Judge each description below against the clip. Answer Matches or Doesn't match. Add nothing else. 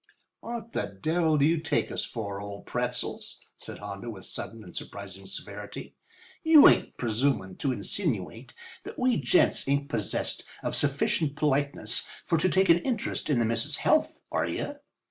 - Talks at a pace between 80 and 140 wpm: Doesn't match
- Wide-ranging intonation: Matches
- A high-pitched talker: Doesn't match